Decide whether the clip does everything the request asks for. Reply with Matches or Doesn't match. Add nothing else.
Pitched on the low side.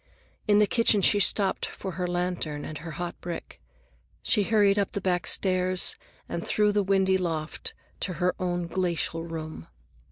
Doesn't match